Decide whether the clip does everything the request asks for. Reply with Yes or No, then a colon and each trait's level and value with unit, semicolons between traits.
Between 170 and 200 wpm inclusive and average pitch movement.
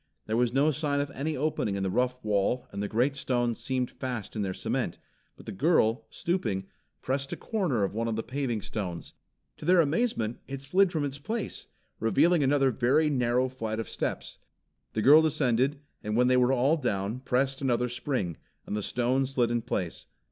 Yes: average, 195 wpm; average, 4.0 semitones